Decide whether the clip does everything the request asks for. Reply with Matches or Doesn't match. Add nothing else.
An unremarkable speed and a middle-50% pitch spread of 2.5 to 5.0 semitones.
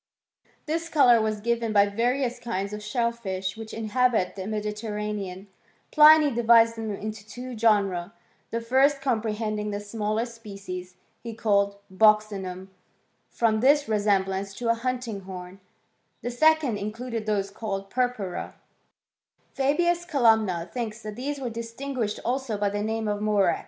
Matches